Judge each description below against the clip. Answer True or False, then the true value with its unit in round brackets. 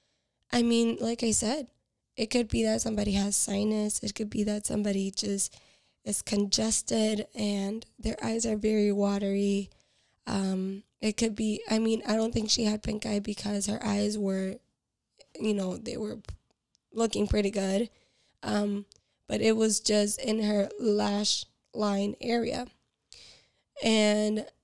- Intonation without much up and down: True (1.5 semitones)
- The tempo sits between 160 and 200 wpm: False (150 wpm)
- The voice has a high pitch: True (215 Hz)